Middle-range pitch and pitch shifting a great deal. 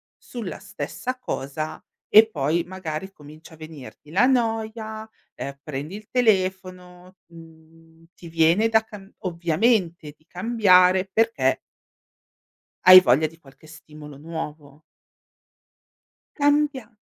Yes: medium, 180 Hz; wide, 5.7 semitones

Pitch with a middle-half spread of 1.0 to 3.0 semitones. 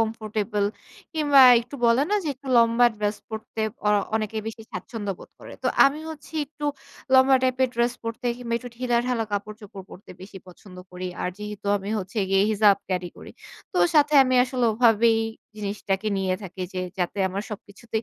No: average, 3.5 semitones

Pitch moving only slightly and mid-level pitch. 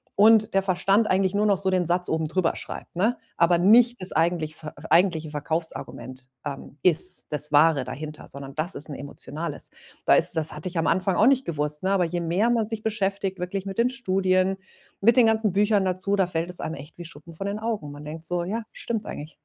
No: average, 4.1 semitones; medium, 180 Hz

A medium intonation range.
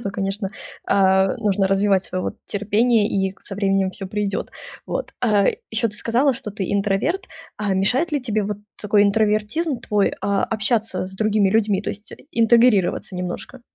No: narrow, 2.3 semitones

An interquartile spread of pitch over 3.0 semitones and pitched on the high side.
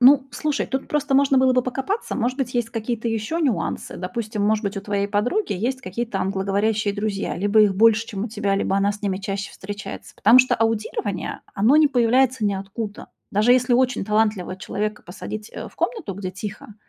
Yes: average, 4.0 semitones; high, 215 Hz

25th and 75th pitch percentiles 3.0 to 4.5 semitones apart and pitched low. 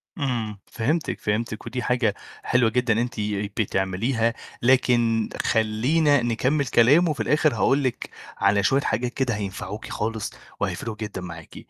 Yes: average, 3.3 semitones; low, 115 Hz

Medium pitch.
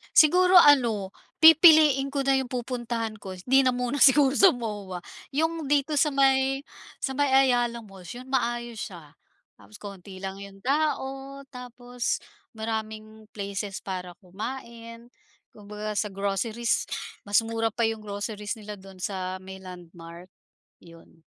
No: high, 230 Hz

